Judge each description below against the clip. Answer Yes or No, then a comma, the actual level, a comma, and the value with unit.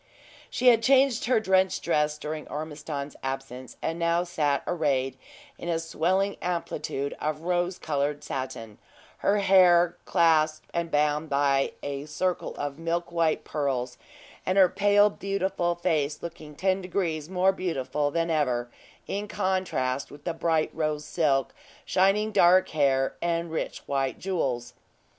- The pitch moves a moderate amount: Yes, average, 4.1 semitones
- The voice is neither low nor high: Yes, medium, 165 Hz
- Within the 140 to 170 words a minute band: Yes, average, 145 wpm